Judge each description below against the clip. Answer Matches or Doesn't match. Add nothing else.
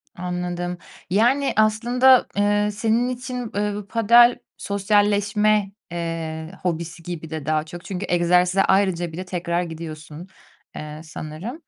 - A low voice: Doesn't match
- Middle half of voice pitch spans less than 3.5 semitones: Doesn't match